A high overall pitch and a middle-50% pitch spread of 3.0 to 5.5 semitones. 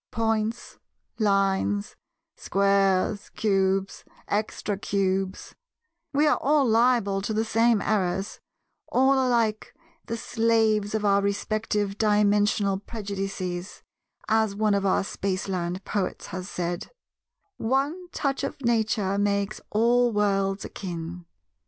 No: high, 205 Hz; narrow, 2.5 semitones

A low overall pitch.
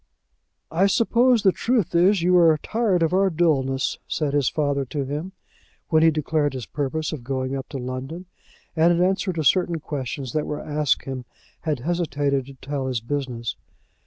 No: medium, 150 Hz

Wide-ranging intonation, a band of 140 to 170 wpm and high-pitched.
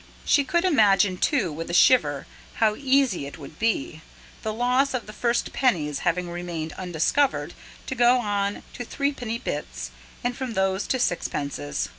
Yes: wide, 6.8 semitones; average, 160 wpm; high, 205 Hz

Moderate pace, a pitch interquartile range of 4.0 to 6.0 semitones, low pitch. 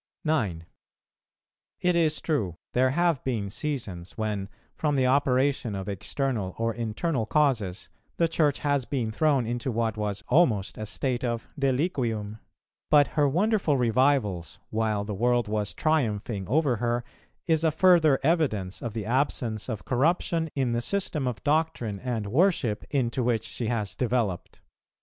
Yes: average, 150 wpm; average, 5.2 semitones; low, 120 Hz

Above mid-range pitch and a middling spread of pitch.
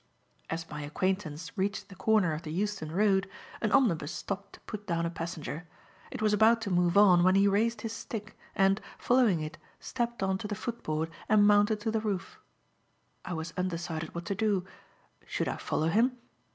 Yes: high, 195 Hz; average, 4.2 semitones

